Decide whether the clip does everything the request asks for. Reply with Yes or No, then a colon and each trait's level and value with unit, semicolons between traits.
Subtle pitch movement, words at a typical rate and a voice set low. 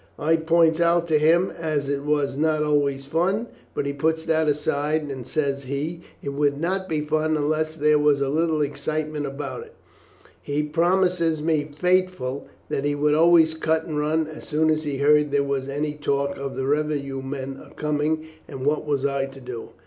No: narrow, 2.1 semitones; average, 195 wpm; medium, 150 Hz